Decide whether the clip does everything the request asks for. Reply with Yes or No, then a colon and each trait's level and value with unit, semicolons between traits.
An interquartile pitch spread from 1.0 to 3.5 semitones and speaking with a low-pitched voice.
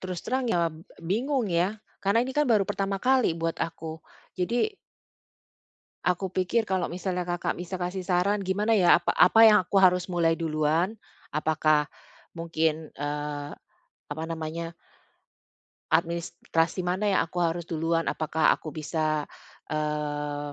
No: average, 3.2 semitones; medium, 170 Hz